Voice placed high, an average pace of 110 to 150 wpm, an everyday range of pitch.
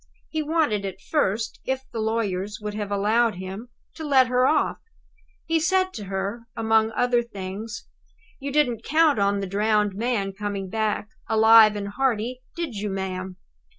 No: high, 220 Hz; average, 160 wpm; average, 3.8 semitones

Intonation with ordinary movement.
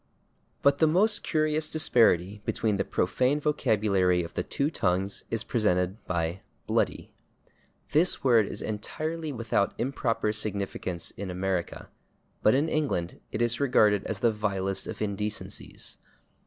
No: wide, 6.4 semitones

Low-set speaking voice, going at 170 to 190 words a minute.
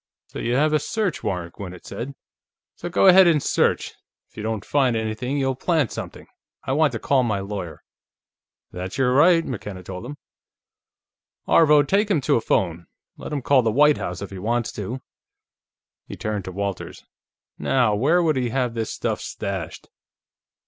Yes: low, 120 Hz; average, 175 wpm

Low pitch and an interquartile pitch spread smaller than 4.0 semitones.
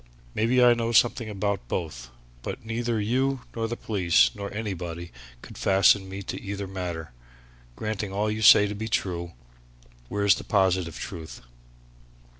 Yes: low, 100 Hz; average, 3.4 semitones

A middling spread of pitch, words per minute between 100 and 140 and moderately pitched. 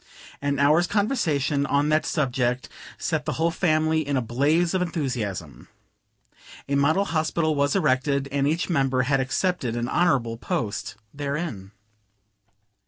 Yes: average, 3.7 semitones; slow, 135 wpm; medium, 145 Hz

